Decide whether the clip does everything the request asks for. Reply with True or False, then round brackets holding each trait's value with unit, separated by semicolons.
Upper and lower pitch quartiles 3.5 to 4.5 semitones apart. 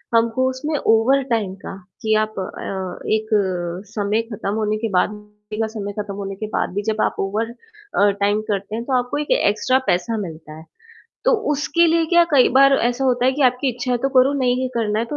True (3.9 semitones)